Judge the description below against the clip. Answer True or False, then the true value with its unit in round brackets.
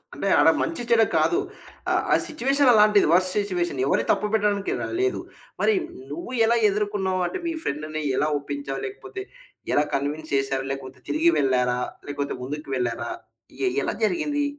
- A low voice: False (185 Hz)